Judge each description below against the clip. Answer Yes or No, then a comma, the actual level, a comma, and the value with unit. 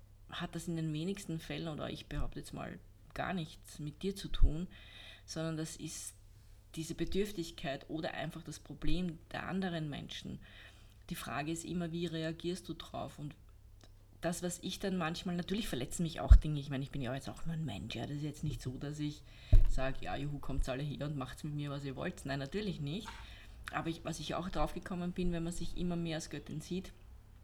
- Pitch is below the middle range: No, medium, 155 Hz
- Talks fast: Yes, fast, 215 wpm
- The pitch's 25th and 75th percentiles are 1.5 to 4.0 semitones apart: No, average, 4.5 semitones